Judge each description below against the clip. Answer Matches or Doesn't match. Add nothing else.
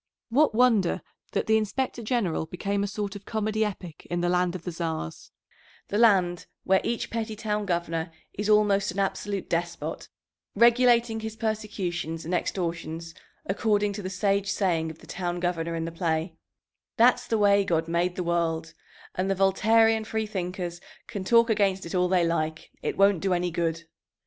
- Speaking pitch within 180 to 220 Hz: Matches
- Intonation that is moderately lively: Matches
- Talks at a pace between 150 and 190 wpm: Matches